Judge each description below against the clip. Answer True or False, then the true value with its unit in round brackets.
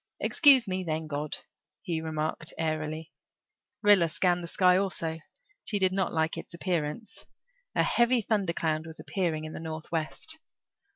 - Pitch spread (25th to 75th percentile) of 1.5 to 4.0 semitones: True (3.3 semitones)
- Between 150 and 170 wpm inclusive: False (140 wpm)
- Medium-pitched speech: True (165 Hz)